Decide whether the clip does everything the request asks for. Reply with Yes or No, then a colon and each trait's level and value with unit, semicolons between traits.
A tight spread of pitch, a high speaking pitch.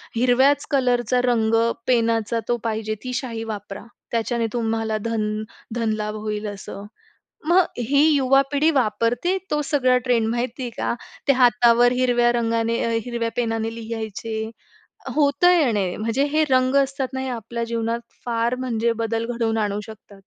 Yes: narrow, 2.2 semitones; high, 235 Hz